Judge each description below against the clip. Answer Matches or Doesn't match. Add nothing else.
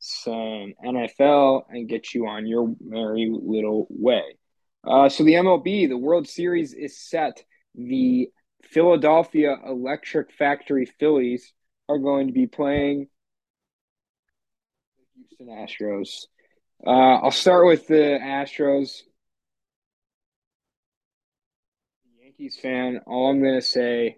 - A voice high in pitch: Doesn't match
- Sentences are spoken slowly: Matches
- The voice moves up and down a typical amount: Matches